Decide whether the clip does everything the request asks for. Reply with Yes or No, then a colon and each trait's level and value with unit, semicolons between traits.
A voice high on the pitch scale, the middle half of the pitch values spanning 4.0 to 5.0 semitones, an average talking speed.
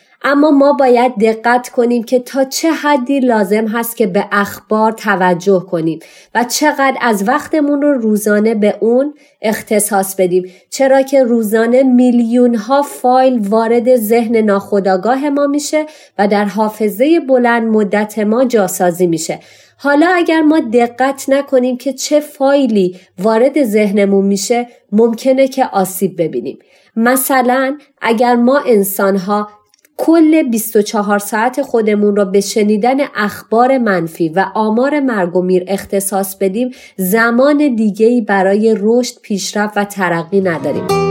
Yes: high, 230 Hz; average, 4.5 semitones; average, 130 wpm